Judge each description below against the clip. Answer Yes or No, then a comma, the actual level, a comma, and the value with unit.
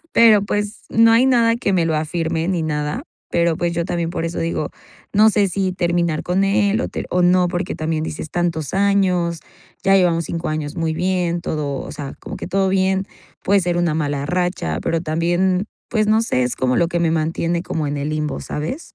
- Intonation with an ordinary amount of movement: Yes, average, 3.3 semitones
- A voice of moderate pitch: Yes, medium, 175 Hz